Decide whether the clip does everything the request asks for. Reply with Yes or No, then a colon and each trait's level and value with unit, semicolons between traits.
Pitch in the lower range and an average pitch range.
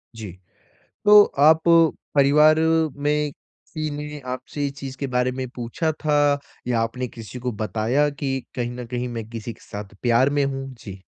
Yes: low, 130 Hz; average, 3.5 semitones